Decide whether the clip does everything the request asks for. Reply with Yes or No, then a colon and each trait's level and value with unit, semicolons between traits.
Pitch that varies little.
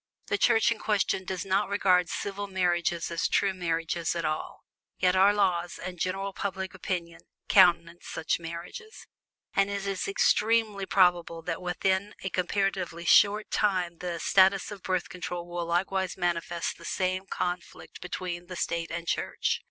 Yes: narrow, 2.3 semitones